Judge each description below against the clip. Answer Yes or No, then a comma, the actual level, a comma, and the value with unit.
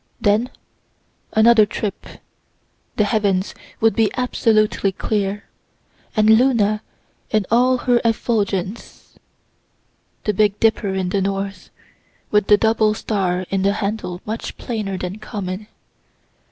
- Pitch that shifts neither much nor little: No, narrow, 2.1 semitones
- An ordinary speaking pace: No, slow, 115 wpm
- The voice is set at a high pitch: Yes, high, 210 Hz